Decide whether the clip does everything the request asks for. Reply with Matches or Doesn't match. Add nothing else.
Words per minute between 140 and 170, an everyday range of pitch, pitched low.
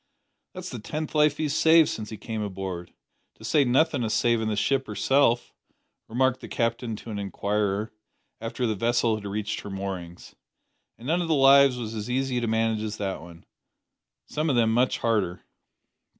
Doesn't match